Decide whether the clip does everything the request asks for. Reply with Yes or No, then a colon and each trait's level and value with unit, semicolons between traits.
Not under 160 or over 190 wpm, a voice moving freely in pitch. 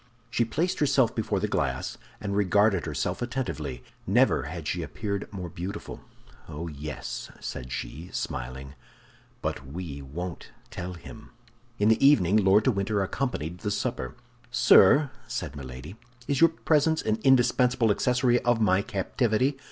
No: average, 145 wpm; wide, 7.0 semitones